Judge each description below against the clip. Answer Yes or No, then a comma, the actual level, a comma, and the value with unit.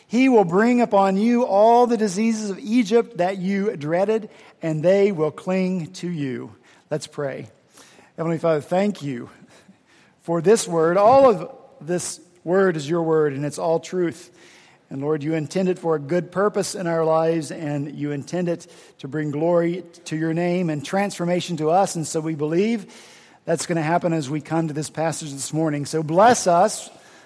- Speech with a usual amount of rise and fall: Yes, average, 3.6 semitones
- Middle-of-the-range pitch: Yes, medium, 170 Hz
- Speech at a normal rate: Yes, average, 185 wpm